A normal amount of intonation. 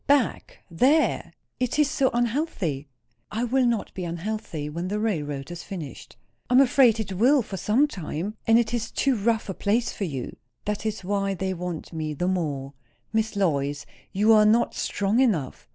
No: wide, 5.7 semitones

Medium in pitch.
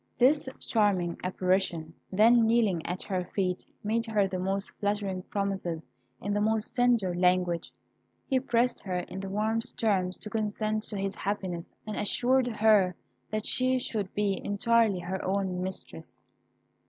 No: high, 200 Hz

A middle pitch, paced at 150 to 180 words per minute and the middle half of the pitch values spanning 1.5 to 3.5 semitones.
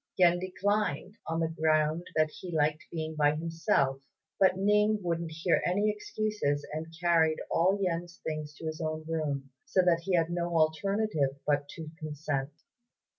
Yes: medium, 165 Hz; average, 160 wpm; average, 2.8 semitones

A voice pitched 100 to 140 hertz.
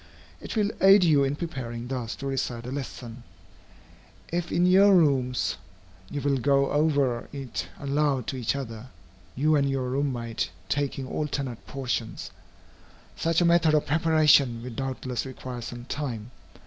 Yes: low, 135 Hz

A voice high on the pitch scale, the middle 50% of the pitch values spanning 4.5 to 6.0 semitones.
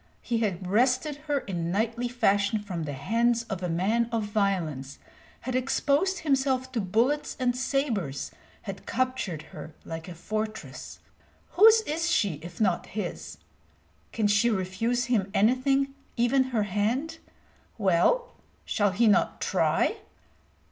Yes: high, 225 Hz; average, 5.3 semitones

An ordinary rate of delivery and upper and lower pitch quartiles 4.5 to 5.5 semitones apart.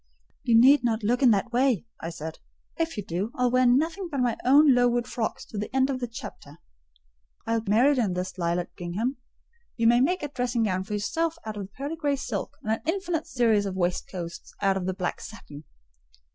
No: fast, 215 wpm; average, 5.2 semitones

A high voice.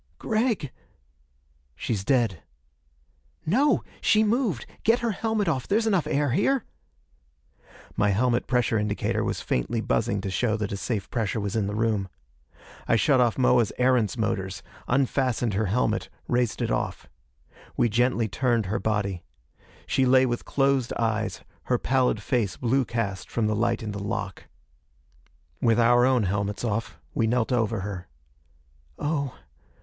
No: low, 120 Hz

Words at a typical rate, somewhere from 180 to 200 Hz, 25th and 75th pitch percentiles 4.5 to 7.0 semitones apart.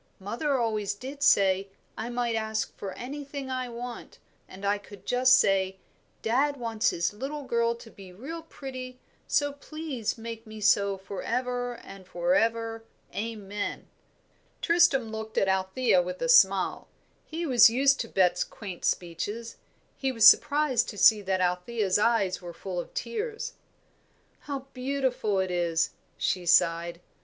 No: average, 150 wpm; high, 225 Hz; average, 5.0 semitones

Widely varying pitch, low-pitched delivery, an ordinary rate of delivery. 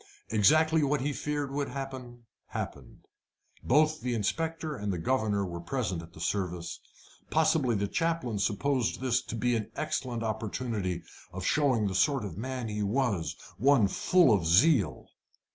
Yes: wide, 5.9 semitones; low, 120 Hz; average, 155 wpm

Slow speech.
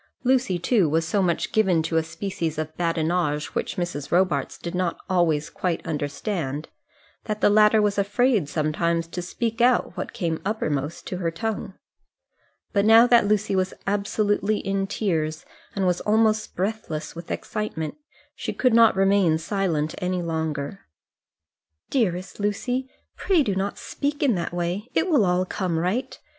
No: average, 155 wpm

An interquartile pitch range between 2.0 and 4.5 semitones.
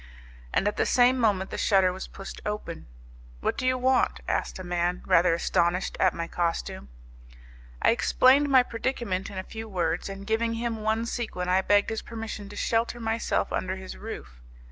Yes: average, 3.9 semitones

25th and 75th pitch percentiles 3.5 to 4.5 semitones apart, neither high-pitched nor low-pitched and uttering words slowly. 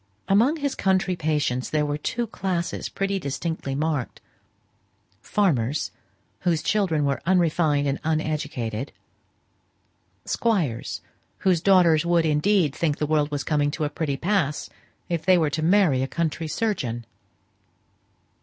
Yes: average, 4.2 semitones; medium, 155 Hz; slow, 130 wpm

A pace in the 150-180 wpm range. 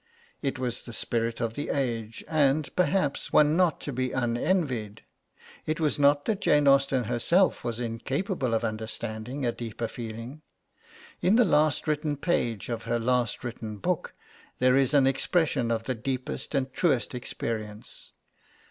Yes: average, 155 wpm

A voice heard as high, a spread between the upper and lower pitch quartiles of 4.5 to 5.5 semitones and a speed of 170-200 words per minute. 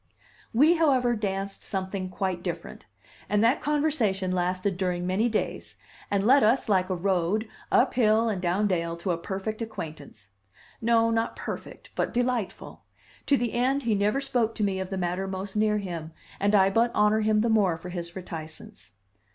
No: high, 200 Hz; average, 3.8 semitones; average, 175 wpm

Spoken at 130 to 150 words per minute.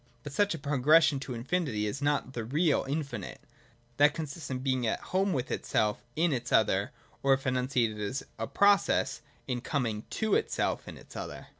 No: average, 180 wpm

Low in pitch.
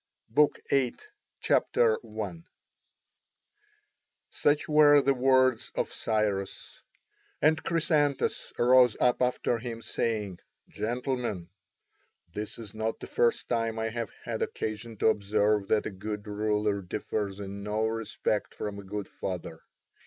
Yes: low, 110 Hz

